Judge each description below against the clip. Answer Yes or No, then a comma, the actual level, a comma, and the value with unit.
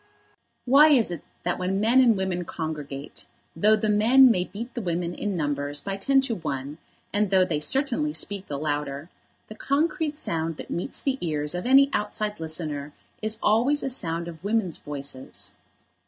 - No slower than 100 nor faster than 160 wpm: No, average, 175 wpm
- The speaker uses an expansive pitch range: Yes, wide, 6.9 semitones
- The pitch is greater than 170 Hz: Yes, high, 190 Hz